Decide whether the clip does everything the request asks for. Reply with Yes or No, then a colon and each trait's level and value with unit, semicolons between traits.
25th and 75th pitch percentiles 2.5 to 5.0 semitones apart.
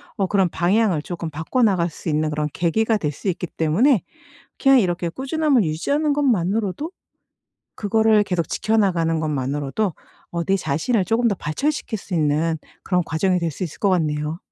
No: wide, 5.5 semitones